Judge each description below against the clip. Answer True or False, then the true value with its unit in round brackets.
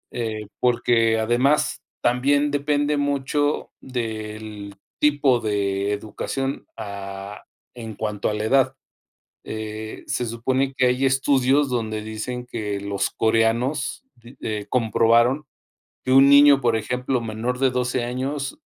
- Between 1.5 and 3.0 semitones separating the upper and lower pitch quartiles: False (3.6 semitones)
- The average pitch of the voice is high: False (120 Hz)